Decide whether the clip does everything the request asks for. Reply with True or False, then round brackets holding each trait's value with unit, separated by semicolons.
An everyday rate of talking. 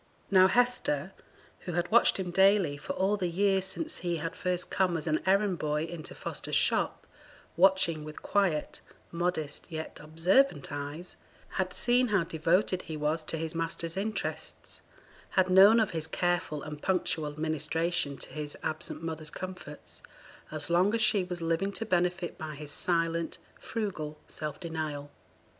True (155 wpm)